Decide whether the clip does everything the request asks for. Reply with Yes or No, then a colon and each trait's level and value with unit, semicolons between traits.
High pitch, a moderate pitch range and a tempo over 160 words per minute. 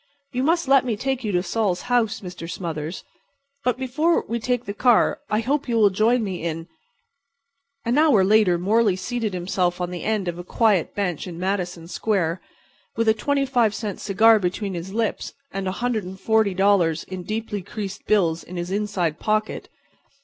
Yes: high, 205 Hz; average, 4.2 semitones; average, 175 wpm